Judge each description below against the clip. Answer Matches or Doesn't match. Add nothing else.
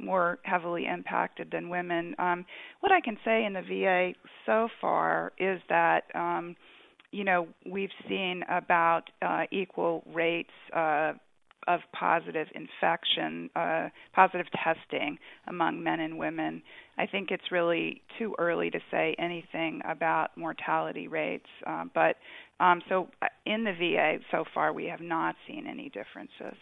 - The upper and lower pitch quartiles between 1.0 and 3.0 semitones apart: Matches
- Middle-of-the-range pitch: Matches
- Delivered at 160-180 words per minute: Doesn't match